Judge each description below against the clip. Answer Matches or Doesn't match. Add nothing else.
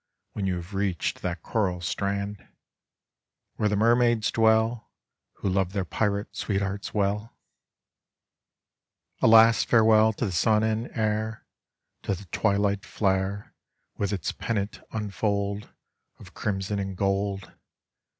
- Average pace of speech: Doesn't match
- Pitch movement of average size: Doesn't match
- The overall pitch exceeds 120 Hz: Doesn't match